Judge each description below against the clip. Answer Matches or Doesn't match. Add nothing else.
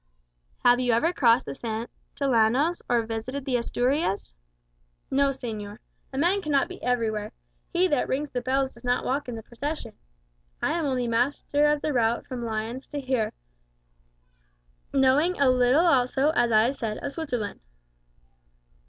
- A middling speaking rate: Matches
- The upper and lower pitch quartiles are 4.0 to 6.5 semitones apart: Doesn't match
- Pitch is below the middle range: Doesn't match